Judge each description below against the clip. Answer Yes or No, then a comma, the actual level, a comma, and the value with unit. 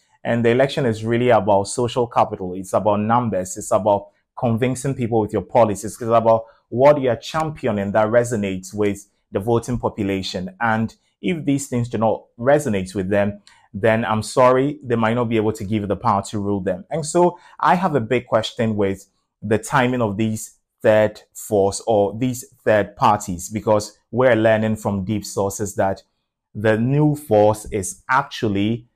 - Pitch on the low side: Yes, low, 110 Hz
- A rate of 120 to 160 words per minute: No, average, 175 wpm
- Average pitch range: Yes, average, 3.2 semitones